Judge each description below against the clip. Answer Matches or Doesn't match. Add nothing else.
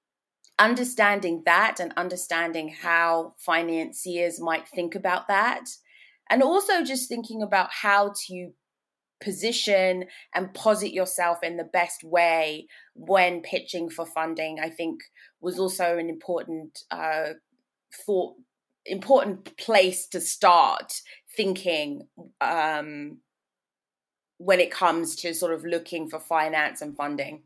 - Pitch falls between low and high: Matches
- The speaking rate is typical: Doesn't match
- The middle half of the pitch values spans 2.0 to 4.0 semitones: Matches